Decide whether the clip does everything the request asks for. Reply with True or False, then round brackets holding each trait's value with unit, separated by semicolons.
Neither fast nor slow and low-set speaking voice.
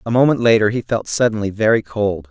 False (210 wpm; 110 Hz)